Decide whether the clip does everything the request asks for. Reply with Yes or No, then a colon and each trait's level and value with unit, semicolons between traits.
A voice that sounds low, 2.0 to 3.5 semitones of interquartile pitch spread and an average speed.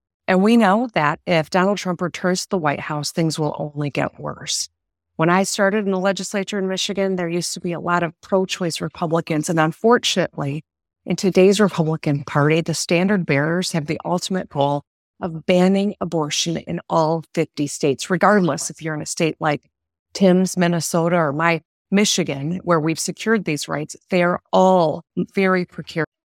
No: medium, 170 Hz; average, 3.2 semitones; average, 175 wpm